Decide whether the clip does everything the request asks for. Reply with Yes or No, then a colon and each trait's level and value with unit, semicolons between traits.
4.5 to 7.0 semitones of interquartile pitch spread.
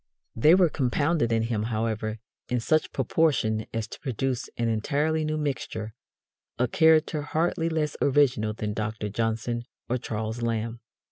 Yes: wide, 5.4 semitones